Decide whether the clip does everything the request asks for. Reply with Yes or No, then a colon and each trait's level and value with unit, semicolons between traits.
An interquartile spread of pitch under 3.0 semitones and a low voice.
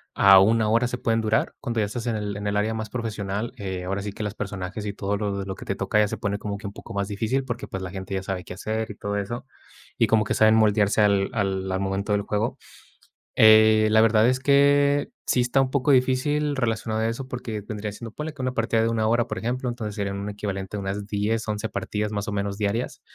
Yes: narrow, 2.4 semitones; low, 110 Hz